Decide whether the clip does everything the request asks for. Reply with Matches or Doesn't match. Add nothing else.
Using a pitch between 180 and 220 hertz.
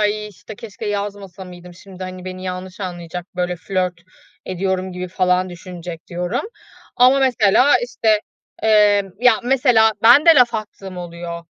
Matches